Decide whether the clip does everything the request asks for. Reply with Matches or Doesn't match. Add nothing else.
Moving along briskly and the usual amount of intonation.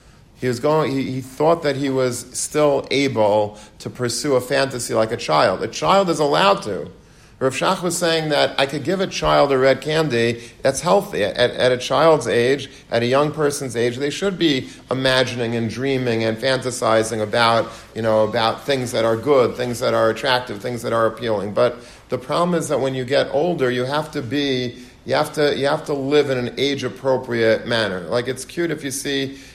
Matches